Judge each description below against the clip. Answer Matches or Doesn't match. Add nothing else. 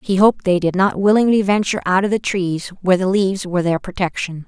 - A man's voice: Doesn't match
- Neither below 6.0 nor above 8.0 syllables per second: Matches